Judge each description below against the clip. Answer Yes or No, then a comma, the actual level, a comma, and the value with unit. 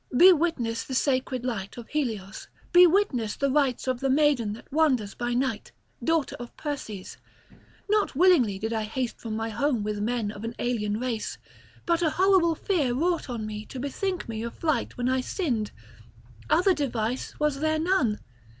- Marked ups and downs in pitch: Yes, wide, 5.7 semitones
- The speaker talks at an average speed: Yes, average, 175 wpm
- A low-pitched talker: No, very high, 255 Hz